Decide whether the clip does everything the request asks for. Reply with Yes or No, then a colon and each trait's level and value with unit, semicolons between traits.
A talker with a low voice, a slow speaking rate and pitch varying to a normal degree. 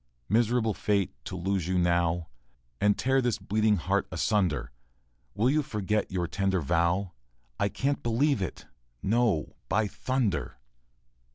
Yes: low, 100 Hz; slow, 130 wpm; average, 4.5 semitones